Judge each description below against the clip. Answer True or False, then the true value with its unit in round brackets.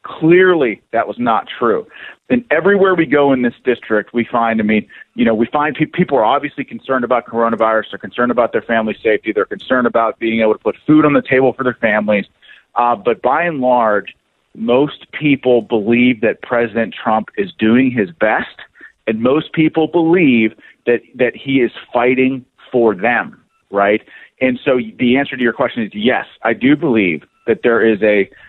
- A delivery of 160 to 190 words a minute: True (185 wpm)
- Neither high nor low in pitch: False (125 Hz)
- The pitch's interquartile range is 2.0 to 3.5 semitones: False (4.2 semitones)